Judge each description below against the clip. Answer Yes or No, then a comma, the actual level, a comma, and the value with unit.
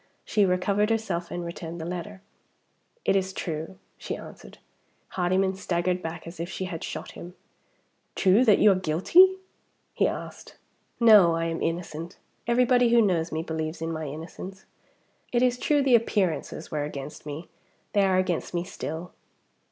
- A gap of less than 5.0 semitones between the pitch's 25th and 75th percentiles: Yes, average, 3.7 semitones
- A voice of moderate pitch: Yes, medium, 180 Hz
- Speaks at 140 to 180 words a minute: Yes, average, 160 wpm